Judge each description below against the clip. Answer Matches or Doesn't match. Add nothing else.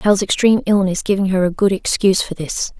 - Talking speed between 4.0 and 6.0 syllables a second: Doesn't match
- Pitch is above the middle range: Matches